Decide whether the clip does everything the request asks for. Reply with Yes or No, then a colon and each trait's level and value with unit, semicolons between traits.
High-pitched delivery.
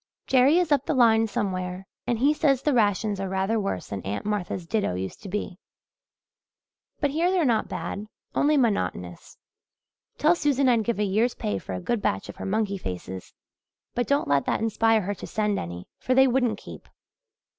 Yes: high, 215 Hz